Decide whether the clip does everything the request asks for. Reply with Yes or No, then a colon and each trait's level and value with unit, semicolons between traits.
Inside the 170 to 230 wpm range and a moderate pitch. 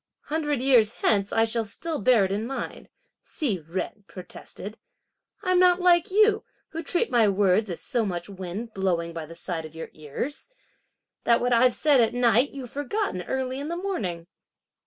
No: average, 180 wpm; high, 235 Hz